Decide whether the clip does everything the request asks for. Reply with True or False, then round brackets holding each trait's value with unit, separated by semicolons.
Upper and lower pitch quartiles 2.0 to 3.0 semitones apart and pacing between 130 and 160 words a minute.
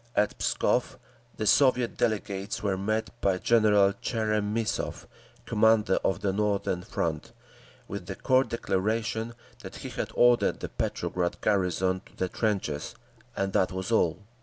True (2.6 semitones; 135 wpm)